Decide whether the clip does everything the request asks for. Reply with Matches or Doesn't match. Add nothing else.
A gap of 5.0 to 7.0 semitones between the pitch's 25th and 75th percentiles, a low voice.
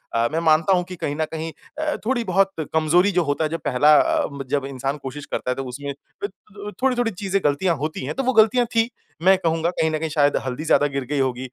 Doesn't match